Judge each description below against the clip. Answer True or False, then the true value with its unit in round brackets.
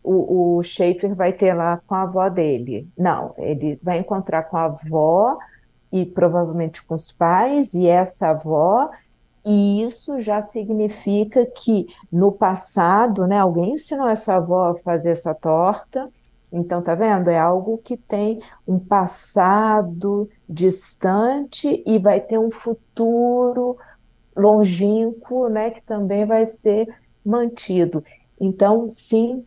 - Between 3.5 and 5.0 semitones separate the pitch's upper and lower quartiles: True (4.2 semitones)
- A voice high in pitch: True (200 Hz)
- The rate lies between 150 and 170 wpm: False (130 wpm)